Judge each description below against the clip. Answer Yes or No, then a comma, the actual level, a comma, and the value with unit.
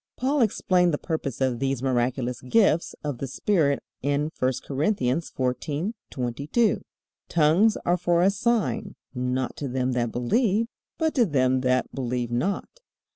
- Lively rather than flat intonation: Yes, wide, 6.7 semitones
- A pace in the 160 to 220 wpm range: No, average, 140 wpm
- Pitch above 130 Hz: Yes, medium, 140 Hz